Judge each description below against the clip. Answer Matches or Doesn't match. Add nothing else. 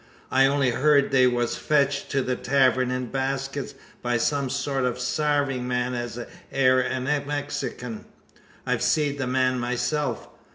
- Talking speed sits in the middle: Matches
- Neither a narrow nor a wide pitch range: Doesn't match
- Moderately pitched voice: Doesn't match